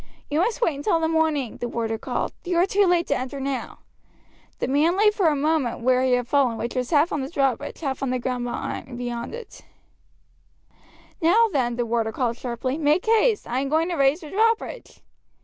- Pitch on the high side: Yes, very high, 280 Hz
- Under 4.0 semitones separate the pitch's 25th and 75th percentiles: No, average, 5.2 semitones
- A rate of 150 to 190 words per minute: No, fast, 205 wpm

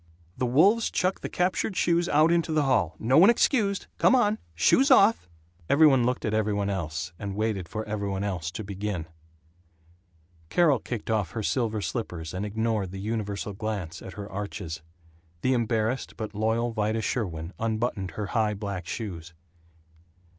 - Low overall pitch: Yes, low, 110 Hz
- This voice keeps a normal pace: Yes, average, 170 wpm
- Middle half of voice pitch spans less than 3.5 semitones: No, average, 4.7 semitones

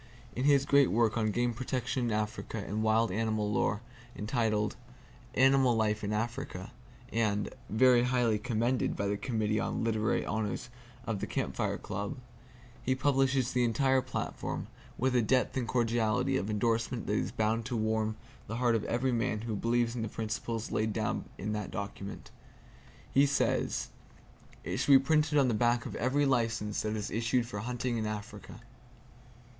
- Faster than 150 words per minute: Yes, average, 170 wpm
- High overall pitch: No, low, 115 Hz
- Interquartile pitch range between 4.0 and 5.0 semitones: No, average, 2.8 semitones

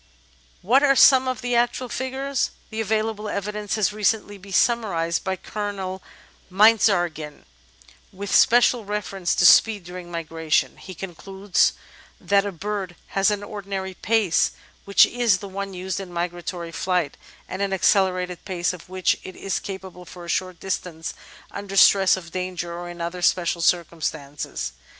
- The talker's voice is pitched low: No, high, 190 Hz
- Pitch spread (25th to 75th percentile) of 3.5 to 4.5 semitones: No, average, 3.0 semitones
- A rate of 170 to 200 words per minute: No, average, 150 wpm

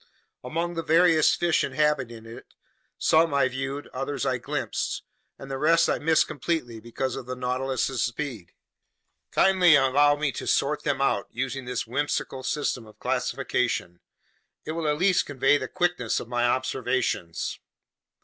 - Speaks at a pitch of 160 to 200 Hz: No, low, 135 Hz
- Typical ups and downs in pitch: Yes, average, 3.6 semitones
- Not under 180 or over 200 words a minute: No, average, 150 wpm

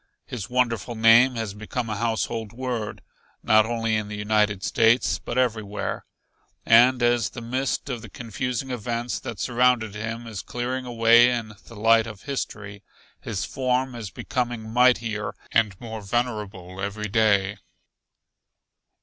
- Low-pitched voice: Yes, low, 115 Hz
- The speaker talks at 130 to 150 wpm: Yes, average, 140 wpm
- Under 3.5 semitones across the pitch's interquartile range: Yes, narrow, 2.4 semitones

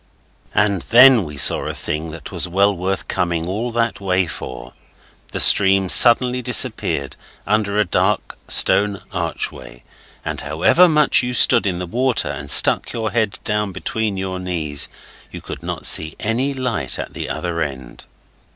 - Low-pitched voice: Yes, very low, 95 Hz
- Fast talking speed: No, average, 160 wpm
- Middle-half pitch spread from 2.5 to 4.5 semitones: No, average, 5.0 semitones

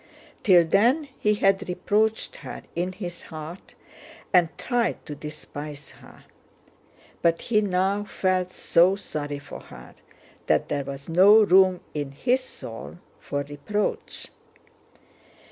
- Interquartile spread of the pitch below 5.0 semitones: No, wide, 5.4 semitones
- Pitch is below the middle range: No, medium, 180 Hz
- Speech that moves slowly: Yes, slow, 125 wpm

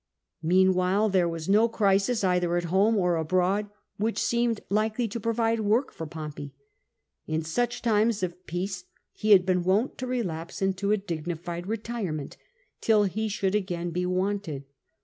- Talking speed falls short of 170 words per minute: Yes, average, 155 wpm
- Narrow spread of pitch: No, average, 3.7 semitones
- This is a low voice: No, high, 195 Hz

